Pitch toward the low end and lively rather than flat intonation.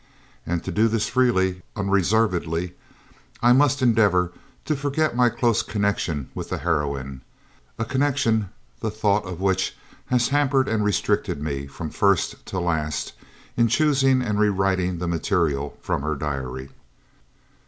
Yes: low, 100 Hz; wide, 6.1 semitones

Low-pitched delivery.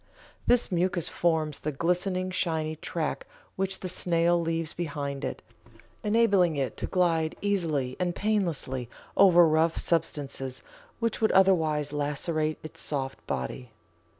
No: medium, 165 Hz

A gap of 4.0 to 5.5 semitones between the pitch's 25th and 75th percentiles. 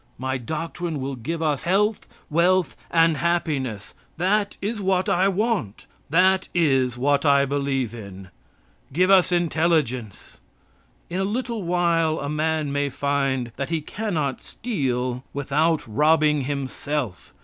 Yes: average, 4.7 semitones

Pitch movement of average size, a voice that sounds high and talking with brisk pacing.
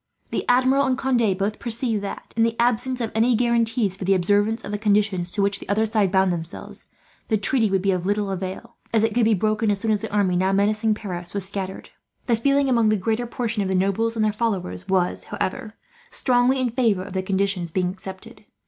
Yes: average, 3.1 semitones; high, 210 Hz; fast, 225 wpm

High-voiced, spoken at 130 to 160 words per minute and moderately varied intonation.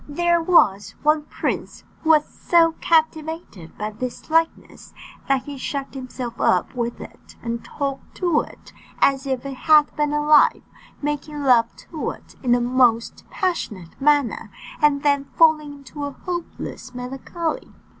Yes: very high, 285 Hz; average, 145 wpm; average, 3.8 semitones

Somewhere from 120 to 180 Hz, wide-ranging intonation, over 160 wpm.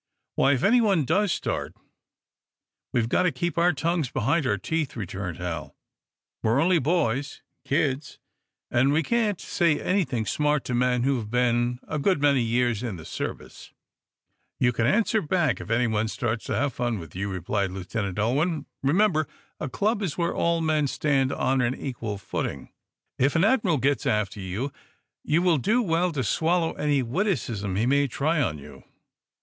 Yes: low, 135 Hz; wide, 6.3 semitones; average, 175 wpm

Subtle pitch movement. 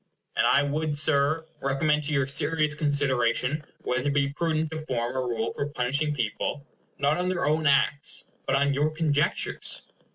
Yes: narrow, 2.0 semitones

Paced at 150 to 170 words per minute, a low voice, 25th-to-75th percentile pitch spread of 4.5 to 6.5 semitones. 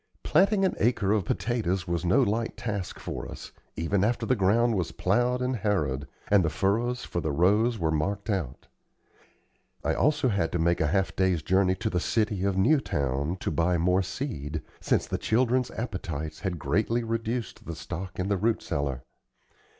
No: average, 180 wpm; very low, 95 Hz; average, 5.2 semitones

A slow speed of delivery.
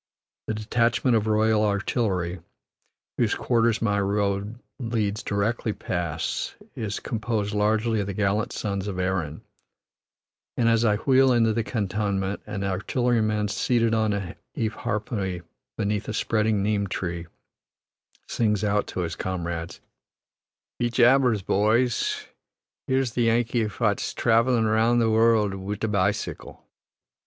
Yes: slow, 130 wpm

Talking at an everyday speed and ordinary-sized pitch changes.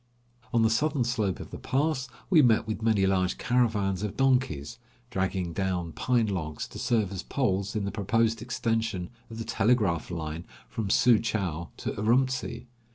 Yes: average, 165 wpm; average, 4.4 semitones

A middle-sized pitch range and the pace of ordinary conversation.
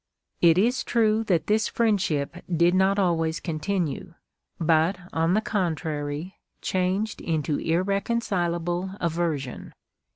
No: average, 3.5 semitones; slow, 120 wpm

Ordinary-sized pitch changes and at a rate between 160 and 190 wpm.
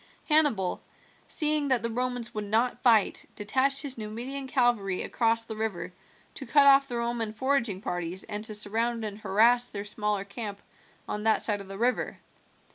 Yes: average, 3.3 semitones; average, 170 wpm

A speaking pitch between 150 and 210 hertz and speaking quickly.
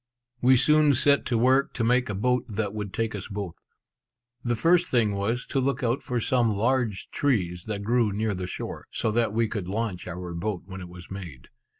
No: low, 110 Hz; fast, 210 wpm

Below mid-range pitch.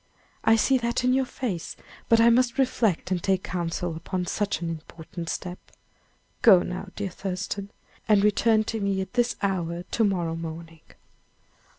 No: high, 195 Hz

